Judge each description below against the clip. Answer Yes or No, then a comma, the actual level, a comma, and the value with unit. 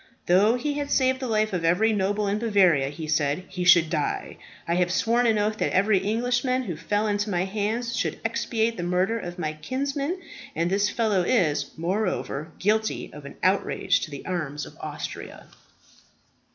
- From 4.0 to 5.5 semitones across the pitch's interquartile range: Yes, average, 4.6 semitones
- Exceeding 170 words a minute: Yes, average, 180 wpm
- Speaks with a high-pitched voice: Yes, high, 200 Hz